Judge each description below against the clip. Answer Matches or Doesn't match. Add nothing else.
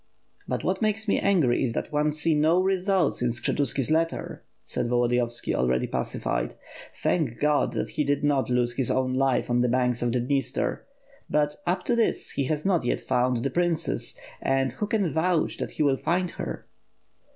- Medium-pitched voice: Matches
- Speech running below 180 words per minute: Doesn't match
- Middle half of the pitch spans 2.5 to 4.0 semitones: Doesn't match